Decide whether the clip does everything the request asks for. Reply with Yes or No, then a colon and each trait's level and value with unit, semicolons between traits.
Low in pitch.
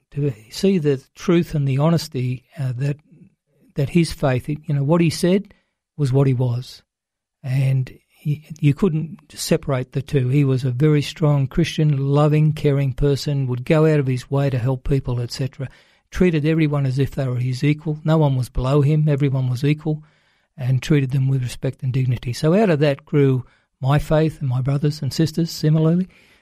No: medium, 145 Hz